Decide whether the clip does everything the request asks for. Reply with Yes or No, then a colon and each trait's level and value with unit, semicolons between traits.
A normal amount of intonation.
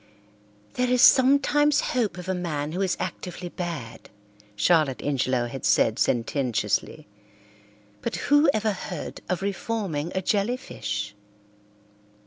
No: wide, 8.7 semitones